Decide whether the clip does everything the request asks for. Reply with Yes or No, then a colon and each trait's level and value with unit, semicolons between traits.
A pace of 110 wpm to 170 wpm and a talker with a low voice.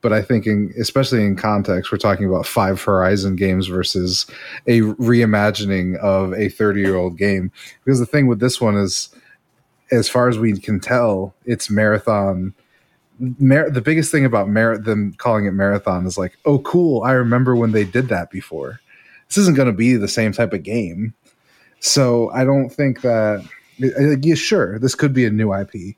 No: average, 185 wpm; low, 110 Hz